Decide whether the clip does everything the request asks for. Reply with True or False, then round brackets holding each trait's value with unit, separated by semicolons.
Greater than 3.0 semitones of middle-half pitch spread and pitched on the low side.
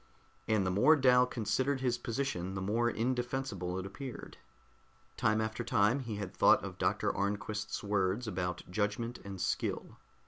True (4.2 semitones; 110 Hz)